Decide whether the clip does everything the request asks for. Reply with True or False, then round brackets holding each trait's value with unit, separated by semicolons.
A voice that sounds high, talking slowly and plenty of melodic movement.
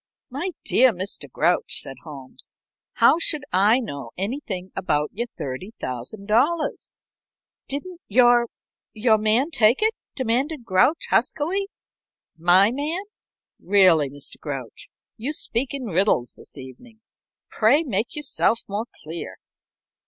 True (220 Hz; 115 wpm; 7.4 semitones)